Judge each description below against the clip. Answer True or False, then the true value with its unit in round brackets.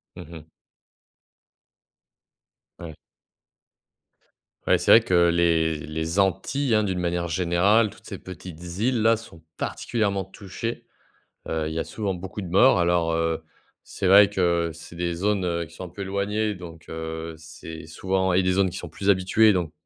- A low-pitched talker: True (90 Hz)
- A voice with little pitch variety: False (3.1 semitones)